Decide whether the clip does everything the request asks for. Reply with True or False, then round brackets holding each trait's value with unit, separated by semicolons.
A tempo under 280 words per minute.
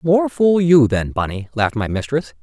True (200 wpm)